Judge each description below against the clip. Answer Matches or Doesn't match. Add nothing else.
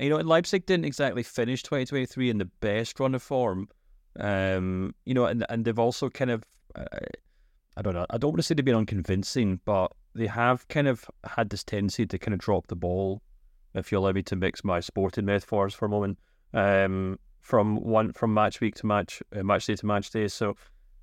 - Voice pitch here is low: Matches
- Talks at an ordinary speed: Doesn't match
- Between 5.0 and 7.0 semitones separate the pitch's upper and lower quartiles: Doesn't match